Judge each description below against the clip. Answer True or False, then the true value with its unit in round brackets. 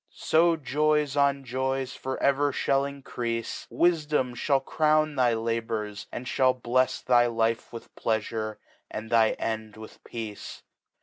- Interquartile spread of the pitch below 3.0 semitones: False (3.7 semitones)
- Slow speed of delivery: True (130 wpm)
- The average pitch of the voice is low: True (130 Hz)